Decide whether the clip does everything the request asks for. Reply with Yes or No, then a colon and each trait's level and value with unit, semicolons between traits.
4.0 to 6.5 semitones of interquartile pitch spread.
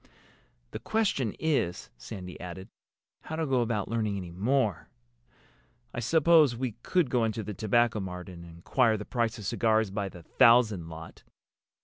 Yes: average, 4.8 semitones